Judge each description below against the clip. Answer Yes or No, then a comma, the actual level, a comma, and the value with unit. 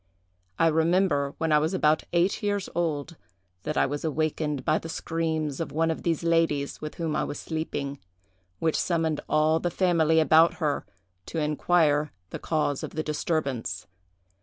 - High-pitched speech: No, medium, 160 Hz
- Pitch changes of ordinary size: No, narrow, 1.7 semitones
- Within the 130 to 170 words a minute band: Yes, average, 165 wpm